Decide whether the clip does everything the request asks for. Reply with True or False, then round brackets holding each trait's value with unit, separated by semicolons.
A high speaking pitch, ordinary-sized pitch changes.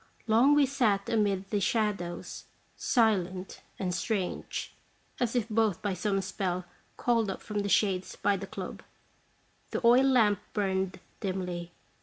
True (200 Hz; 3.2 semitones)